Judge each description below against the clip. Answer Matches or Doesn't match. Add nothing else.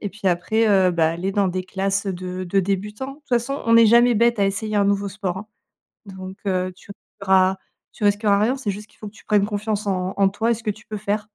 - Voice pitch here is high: Matches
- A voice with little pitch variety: Matches